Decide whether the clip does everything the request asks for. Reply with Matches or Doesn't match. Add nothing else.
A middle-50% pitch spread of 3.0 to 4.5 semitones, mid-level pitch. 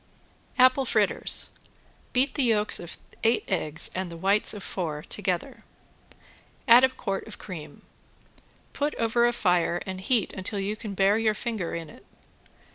Doesn't match